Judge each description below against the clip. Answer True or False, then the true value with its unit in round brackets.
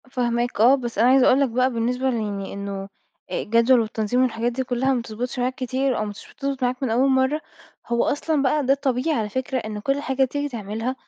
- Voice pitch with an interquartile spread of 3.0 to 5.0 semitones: False (2.6 semitones)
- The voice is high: True (250 Hz)